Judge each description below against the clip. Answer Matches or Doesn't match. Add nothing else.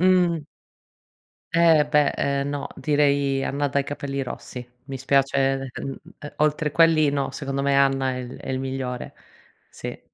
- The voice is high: Doesn't match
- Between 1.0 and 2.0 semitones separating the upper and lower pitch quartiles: Matches